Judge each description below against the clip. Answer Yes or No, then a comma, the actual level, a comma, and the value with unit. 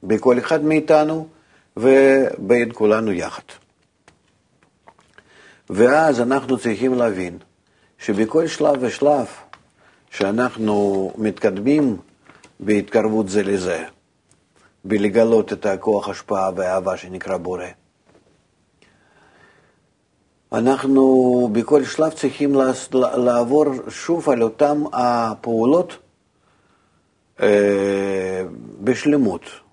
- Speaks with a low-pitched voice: Yes, low, 120 Hz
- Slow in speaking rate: Yes, slow, 70 wpm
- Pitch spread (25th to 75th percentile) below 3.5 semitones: No, average, 4.4 semitones